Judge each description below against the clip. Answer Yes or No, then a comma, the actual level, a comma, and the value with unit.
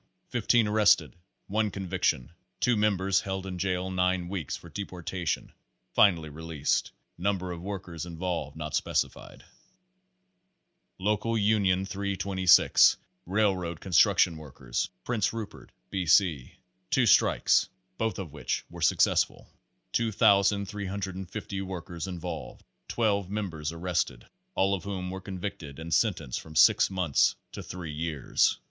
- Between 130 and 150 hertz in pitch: No, very low, 95 Hz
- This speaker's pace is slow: Yes, slow, 120 wpm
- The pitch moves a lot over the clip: No, average, 3.1 semitones